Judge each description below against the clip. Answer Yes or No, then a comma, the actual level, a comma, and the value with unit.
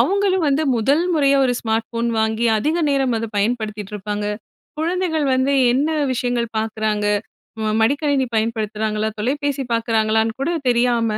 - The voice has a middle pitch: No, high, 235 Hz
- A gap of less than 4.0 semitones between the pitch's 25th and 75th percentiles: No, average, 4.4 semitones